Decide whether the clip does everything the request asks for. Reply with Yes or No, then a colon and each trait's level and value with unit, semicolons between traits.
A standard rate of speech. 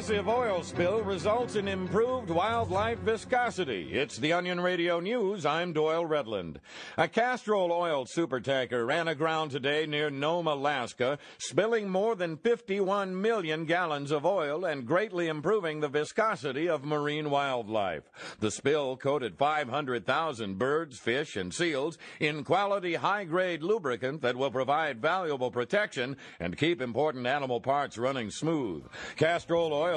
No: slow, 130 wpm